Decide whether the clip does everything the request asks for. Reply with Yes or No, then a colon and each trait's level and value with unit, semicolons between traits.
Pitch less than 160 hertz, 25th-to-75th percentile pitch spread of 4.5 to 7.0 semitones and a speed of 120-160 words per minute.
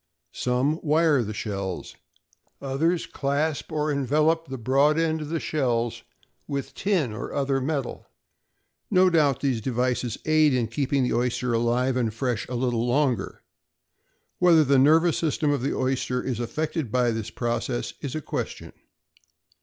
No: low, 135 Hz; average, 3.9 semitones; average, 150 wpm